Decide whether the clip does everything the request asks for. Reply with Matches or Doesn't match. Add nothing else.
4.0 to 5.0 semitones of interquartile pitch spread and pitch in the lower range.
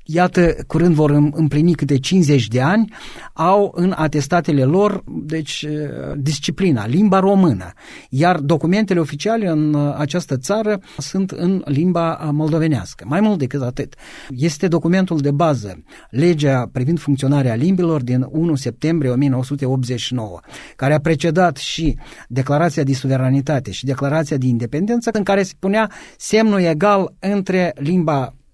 Doesn't match